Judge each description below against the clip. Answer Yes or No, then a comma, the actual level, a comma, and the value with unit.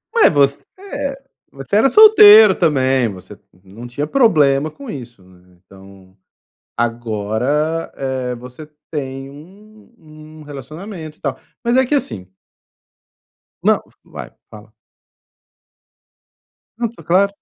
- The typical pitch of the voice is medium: Yes, medium, 145 Hz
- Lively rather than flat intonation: Yes, wide, 8.9 semitones